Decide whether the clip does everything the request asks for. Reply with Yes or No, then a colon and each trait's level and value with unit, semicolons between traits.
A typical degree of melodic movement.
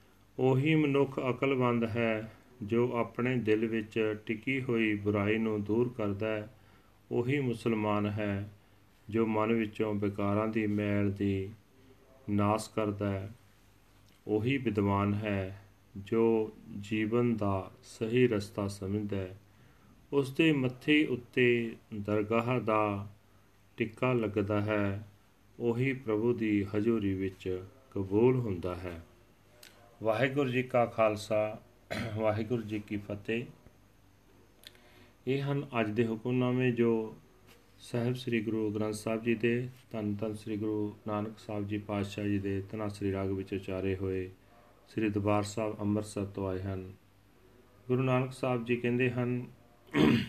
Yes: average, 3.0 semitones